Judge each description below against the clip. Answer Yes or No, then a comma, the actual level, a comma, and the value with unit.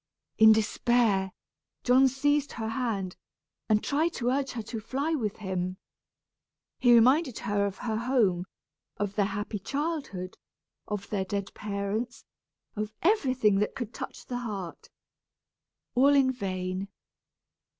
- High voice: Yes, high, 220 Hz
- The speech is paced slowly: Yes, slow, 130 wpm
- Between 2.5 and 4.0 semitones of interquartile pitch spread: No, average, 4.5 semitones